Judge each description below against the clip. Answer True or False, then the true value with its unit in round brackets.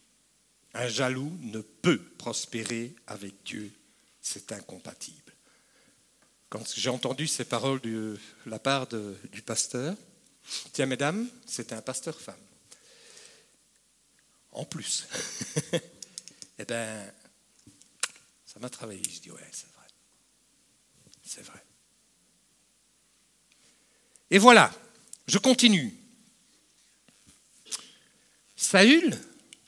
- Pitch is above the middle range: False (140 Hz)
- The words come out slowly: True (90 wpm)